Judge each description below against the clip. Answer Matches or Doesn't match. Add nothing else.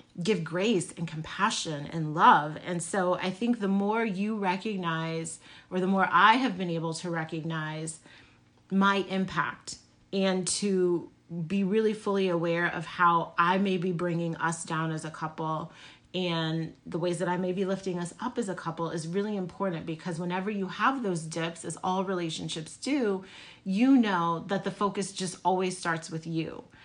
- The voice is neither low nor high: Matches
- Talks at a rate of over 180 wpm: Doesn't match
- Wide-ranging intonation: Doesn't match